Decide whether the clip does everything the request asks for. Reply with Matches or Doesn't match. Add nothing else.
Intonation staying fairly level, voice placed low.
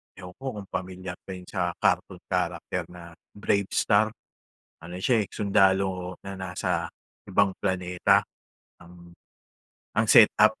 Matches